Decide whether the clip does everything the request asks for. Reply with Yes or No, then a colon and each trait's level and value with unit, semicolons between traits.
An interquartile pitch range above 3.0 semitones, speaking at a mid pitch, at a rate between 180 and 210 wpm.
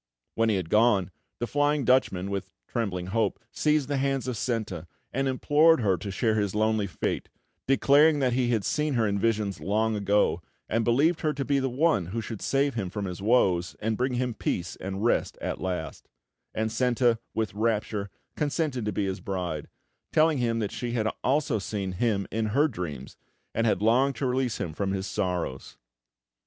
No: average, 4.8 semitones; low, 110 Hz; average, 190 wpm